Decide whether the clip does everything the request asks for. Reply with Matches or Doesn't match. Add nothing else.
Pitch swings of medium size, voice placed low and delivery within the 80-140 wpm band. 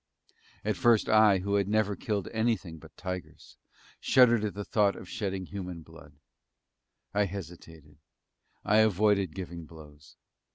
Matches